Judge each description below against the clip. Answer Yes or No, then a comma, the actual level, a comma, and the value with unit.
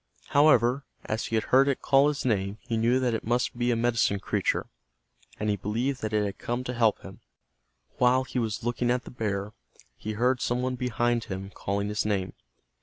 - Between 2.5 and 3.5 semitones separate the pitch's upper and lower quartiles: Yes, average, 2.9 semitones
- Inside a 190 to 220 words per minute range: Yes, fast, 205 wpm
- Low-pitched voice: Yes, low, 120 Hz